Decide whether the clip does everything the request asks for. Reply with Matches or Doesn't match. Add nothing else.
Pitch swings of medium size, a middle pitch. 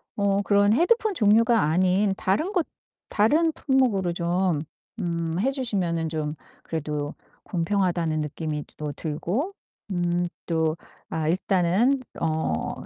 Matches